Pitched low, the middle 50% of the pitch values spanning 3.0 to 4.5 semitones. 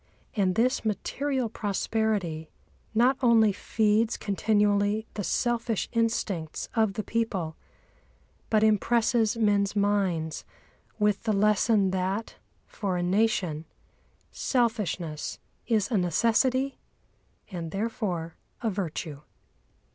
No: high, 210 Hz; average, 3.4 semitones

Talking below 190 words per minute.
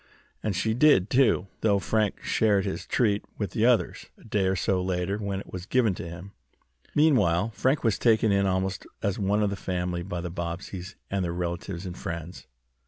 No: average, 195 wpm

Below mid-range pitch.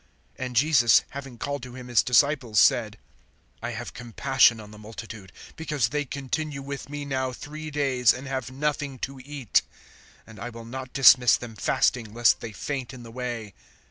Yes: low, 125 Hz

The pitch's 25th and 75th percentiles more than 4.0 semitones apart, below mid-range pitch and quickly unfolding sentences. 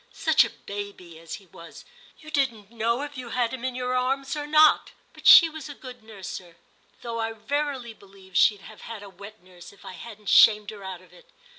No: average, 4.6 semitones; high, 225 Hz; fast, 220 wpm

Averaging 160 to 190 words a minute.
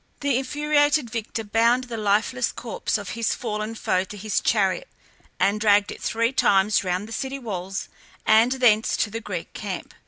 Yes: average, 175 wpm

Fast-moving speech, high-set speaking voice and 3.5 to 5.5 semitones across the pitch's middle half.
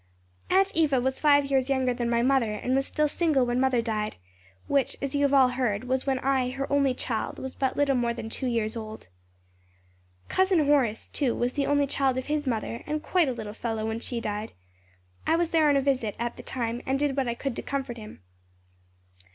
No: fast, 220 wpm; very high, 260 Hz; average, 3.1 semitones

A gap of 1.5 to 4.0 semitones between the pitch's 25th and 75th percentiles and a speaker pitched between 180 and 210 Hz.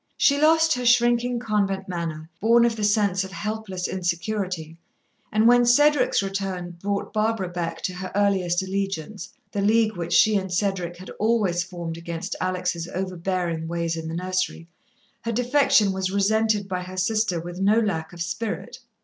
Yes: average, 3.7 semitones; high, 190 Hz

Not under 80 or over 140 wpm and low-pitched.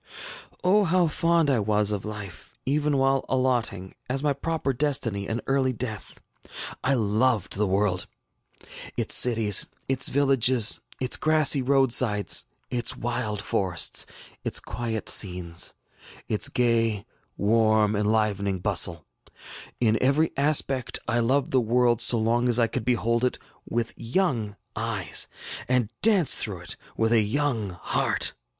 Yes: slow, 135 wpm; low, 120 Hz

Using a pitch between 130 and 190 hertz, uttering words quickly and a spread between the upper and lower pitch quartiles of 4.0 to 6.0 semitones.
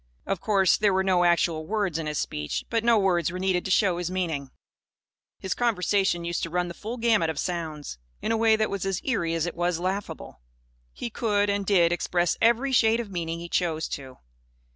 No: medium, 185 Hz; fast, 210 wpm; average, 3.5 semitones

